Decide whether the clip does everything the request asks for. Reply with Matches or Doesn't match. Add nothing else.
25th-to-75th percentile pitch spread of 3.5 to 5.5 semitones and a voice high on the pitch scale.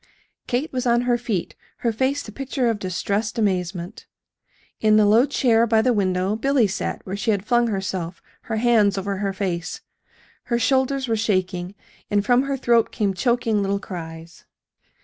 Matches